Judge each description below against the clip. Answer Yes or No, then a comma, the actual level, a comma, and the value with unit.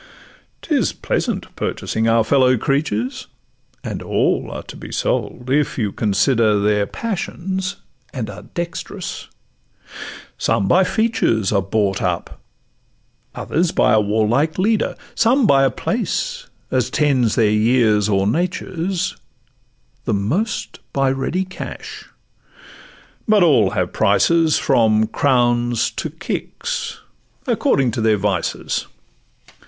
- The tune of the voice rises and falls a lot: Yes, wide, 7.6 semitones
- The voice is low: Yes, low, 125 Hz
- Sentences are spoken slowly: Yes, slow, 115 wpm